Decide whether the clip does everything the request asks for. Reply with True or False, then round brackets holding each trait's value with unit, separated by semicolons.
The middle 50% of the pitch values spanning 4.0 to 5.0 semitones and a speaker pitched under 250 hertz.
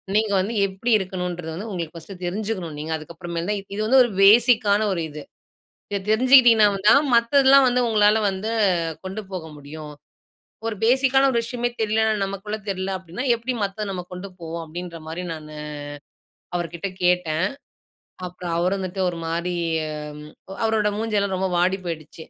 True (4.3 semitones; 190 Hz)